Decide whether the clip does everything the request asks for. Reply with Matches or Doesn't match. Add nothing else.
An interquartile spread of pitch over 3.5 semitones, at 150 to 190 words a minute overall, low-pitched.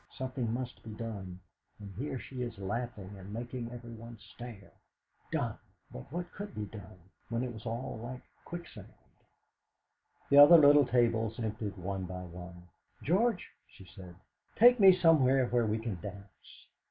Matches